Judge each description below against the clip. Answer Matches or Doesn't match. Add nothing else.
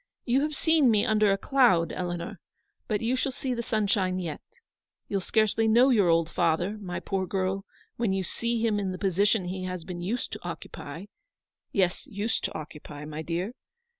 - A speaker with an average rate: Matches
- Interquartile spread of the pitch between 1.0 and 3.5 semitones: Doesn't match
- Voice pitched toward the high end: Matches